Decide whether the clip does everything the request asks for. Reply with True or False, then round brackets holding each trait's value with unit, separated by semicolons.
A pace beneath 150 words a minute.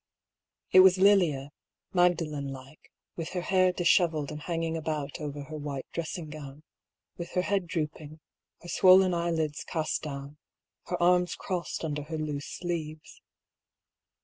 True (140 wpm)